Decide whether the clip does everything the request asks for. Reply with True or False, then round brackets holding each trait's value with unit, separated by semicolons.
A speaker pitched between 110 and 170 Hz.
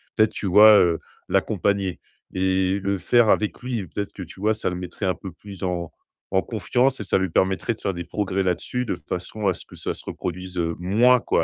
False (95 Hz)